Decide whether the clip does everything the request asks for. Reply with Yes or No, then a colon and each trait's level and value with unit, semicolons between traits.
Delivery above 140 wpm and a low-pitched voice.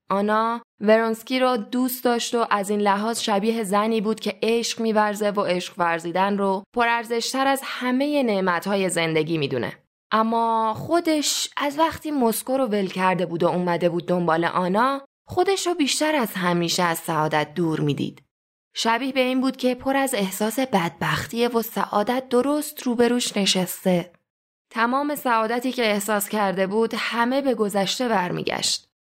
No: average, 150 wpm; high, 220 Hz